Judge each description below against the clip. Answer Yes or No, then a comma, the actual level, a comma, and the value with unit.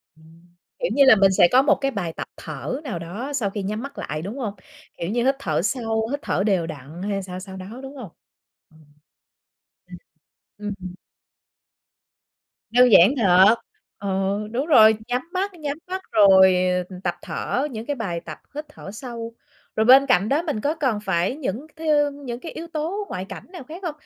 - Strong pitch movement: Yes, wide, 6.7 semitones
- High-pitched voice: Yes, high, 225 Hz